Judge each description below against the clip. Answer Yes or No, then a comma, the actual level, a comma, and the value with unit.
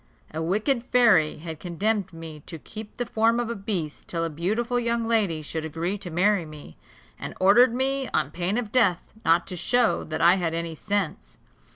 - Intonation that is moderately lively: No, wide, 5.8 semitones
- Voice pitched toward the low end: No, high, 190 Hz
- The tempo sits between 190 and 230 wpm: Yes, average, 195 wpm